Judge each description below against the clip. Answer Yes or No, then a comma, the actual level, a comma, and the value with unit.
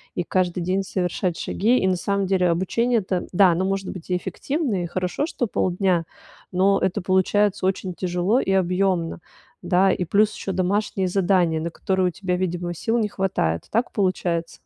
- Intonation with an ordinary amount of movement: No, narrow, 1.8 semitones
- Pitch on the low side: No, medium, 185 Hz